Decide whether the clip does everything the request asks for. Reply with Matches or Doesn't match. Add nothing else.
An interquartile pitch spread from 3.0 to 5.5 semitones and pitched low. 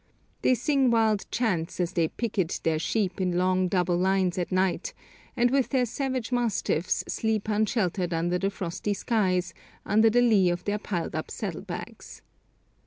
Doesn't match